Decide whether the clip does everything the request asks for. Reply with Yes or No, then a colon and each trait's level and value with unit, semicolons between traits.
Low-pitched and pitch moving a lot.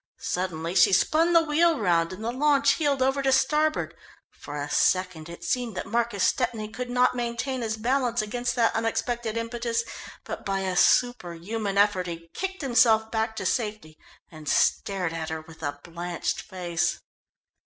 No: high, 220 Hz; wide, 5.8 semitones